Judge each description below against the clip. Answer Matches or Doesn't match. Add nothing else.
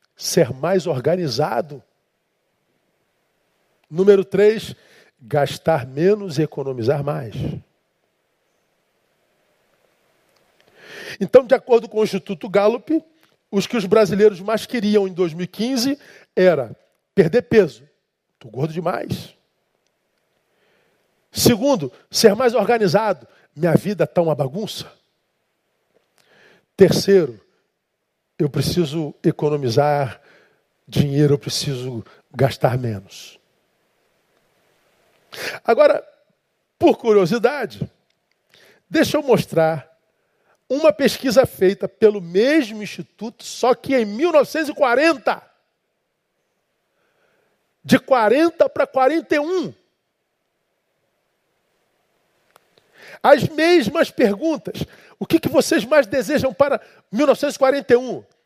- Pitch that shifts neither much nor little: Doesn't match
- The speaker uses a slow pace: Matches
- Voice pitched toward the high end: Matches